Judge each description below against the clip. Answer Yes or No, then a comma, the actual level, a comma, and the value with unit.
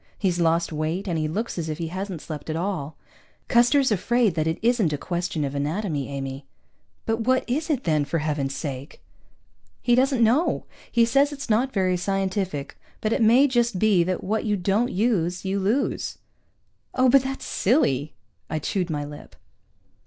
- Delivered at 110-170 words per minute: No, average, 180 wpm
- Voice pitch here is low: No, high, 190 Hz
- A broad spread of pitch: Yes, wide, 7.0 semitones